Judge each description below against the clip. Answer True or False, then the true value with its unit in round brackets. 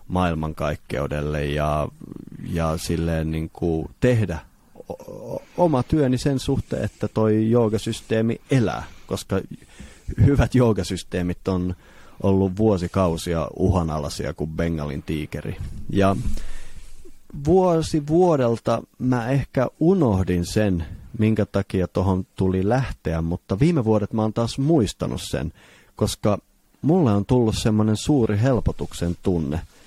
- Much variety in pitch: True (6.0 semitones)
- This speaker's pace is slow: False (105 wpm)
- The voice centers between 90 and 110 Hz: True (100 Hz)